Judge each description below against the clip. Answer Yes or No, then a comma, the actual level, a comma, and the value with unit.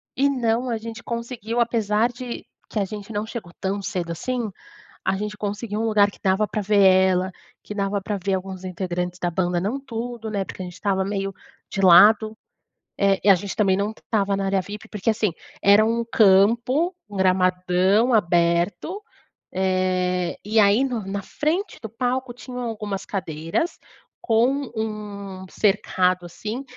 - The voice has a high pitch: Yes, high, 205 Hz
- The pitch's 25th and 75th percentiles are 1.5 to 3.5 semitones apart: Yes, average, 3.2 semitones